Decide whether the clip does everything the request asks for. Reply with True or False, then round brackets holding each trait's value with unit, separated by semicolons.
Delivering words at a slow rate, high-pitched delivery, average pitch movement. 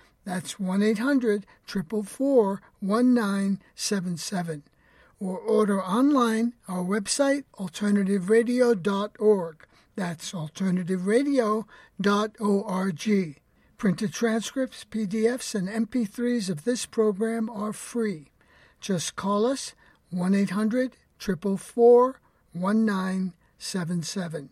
True (70 wpm; 205 Hz; 3.5 semitones)